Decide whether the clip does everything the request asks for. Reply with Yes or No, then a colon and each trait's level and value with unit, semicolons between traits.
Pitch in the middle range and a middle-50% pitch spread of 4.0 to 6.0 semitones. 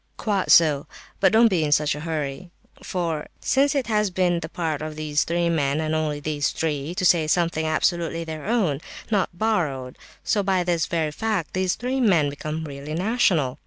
No: medium, 165 Hz; average, 3.6 semitones